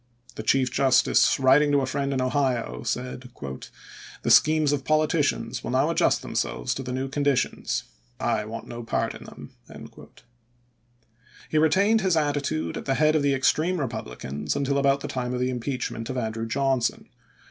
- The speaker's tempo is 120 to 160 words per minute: No, average, 185 wpm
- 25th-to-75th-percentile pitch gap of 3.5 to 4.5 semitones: No, average, 2.7 semitones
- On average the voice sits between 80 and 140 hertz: Yes, low, 135 Hz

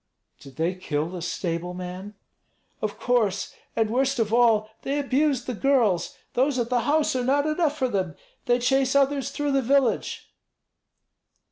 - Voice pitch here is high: Yes, high, 245 Hz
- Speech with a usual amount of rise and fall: No, wide, 6.2 semitones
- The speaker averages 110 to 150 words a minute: No, average, 160 wpm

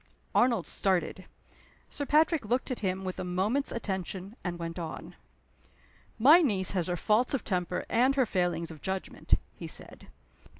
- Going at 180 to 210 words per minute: No, average, 160 wpm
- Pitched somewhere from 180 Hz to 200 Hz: Yes, high, 190 Hz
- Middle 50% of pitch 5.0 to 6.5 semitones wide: Yes, wide, 5.6 semitones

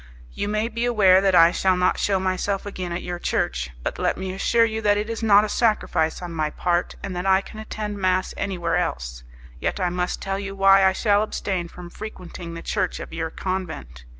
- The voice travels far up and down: No, average, 2.7 semitones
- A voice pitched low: No, high, 190 Hz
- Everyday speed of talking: No, fast, 220 wpm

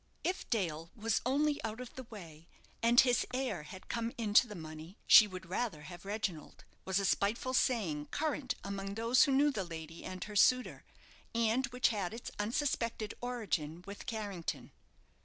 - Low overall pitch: No, high, 215 Hz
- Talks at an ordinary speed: Yes, average, 170 wpm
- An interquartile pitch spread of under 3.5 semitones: No, average, 5.1 semitones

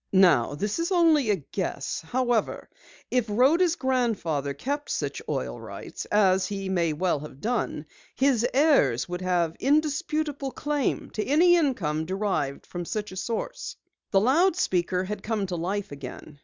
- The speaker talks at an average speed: Yes, average, 145 wpm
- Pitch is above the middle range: Yes, high, 210 Hz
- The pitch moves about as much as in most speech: No, wide, 7.9 semitones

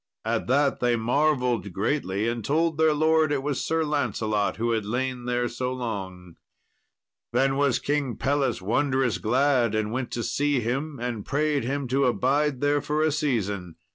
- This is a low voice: Yes, low, 130 Hz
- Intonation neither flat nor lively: Yes, average, 3.9 semitones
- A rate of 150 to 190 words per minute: Yes, average, 170 wpm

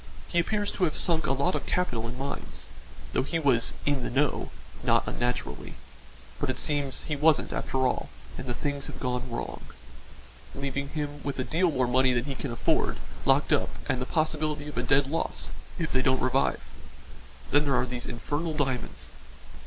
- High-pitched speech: No, medium, 140 Hz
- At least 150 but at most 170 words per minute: No, average, 190 wpm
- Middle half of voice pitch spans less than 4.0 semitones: Yes, average, 2.9 semitones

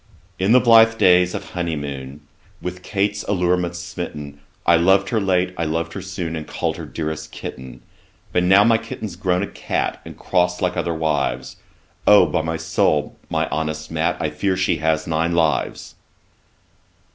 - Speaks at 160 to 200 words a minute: Yes, average, 170 wpm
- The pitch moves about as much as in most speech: Yes, average, 3.2 semitones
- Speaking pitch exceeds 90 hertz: No, very low, 85 Hz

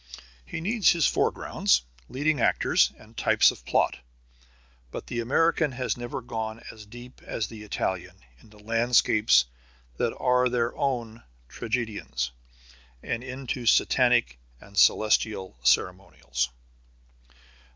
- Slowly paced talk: Yes, slow, 115 wpm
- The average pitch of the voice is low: Yes, low, 115 Hz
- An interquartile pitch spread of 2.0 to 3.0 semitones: No, average, 3.7 semitones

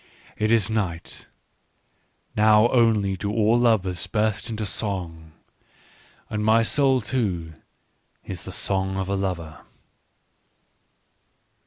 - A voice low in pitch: Yes, low, 105 Hz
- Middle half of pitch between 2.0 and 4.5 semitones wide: Yes, average, 2.9 semitones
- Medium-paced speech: No, slow, 115 wpm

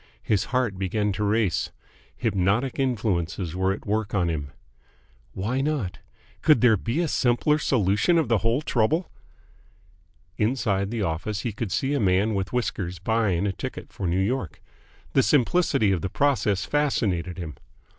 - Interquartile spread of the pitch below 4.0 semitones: No, average, 4.9 semitones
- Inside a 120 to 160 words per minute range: Yes, average, 155 wpm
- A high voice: No, low, 105 Hz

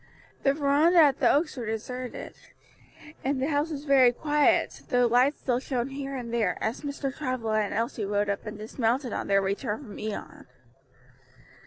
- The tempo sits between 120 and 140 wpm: No, average, 170 wpm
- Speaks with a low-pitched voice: No, very high, 250 Hz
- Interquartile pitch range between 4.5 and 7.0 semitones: No, average, 4.1 semitones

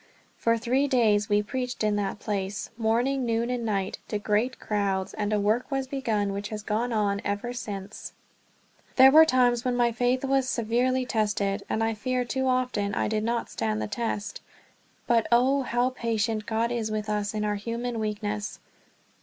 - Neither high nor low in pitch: No, high, 225 Hz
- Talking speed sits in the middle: Yes, average, 180 wpm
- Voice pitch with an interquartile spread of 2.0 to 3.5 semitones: Yes, average, 3.0 semitones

